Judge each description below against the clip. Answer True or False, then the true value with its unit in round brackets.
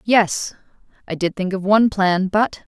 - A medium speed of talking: False (130 wpm)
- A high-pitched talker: True (195 Hz)